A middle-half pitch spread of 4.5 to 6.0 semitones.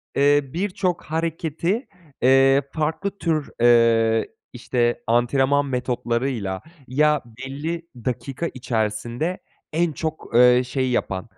Yes: average, 4.8 semitones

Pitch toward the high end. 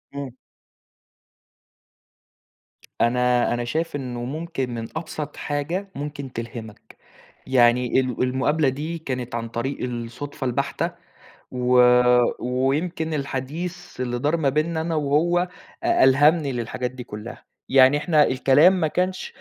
No: low, 135 Hz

